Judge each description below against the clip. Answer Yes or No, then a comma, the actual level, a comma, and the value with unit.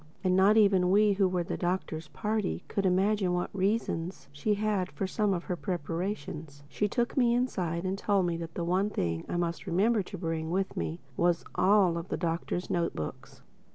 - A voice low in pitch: No, medium, 185 Hz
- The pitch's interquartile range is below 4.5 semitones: Yes, average, 3.2 semitones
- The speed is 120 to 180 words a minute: No, average, 200 wpm